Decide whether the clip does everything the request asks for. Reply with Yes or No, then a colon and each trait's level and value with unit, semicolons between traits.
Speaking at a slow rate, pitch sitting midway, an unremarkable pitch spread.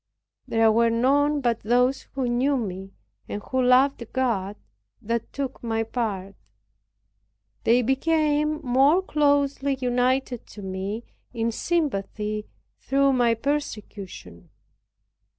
No: slow, 110 wpm; high, 245 Hz; average, 4.0 semitones